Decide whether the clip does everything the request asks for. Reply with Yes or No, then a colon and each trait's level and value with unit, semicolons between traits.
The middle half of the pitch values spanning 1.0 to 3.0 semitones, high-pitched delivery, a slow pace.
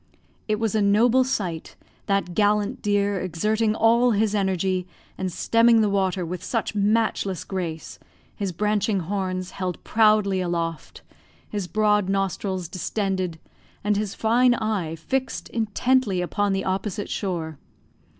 Yes: average, 2.7 semitones; high, 200 Hz; slow, 130 wpm